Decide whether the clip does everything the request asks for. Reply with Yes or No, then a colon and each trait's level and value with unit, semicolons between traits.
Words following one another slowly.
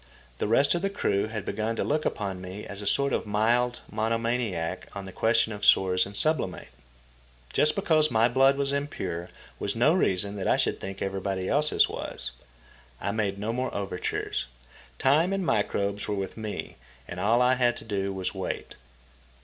No: average, 185 wpm